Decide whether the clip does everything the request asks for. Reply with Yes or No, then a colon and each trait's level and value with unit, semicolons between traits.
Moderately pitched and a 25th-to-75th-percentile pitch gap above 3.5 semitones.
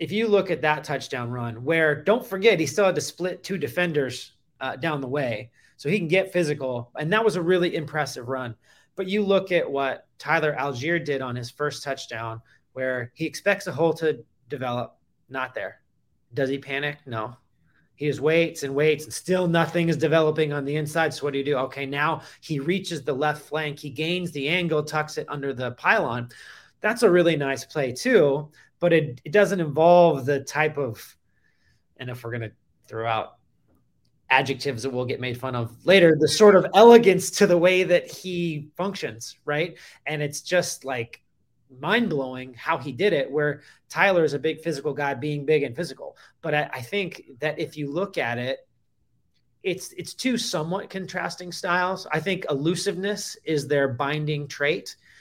Yes: medium, 150 Hz; average, 4.4 semitones